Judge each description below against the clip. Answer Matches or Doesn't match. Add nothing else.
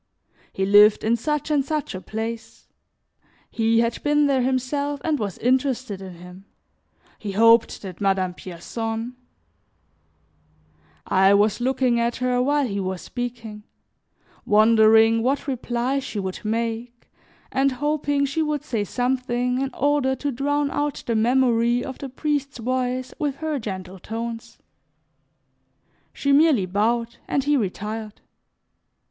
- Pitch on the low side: Doesn't match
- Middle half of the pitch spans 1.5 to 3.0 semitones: Doesn't match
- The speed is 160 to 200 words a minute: Doesn't match